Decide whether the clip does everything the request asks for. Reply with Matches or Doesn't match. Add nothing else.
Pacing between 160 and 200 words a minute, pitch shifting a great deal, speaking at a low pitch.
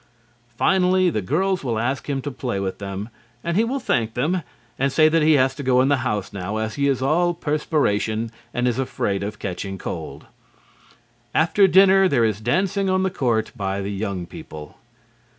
Matches